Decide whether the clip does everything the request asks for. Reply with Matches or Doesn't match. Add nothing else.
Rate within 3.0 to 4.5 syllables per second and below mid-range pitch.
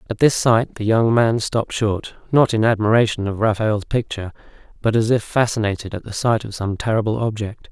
Doesn't match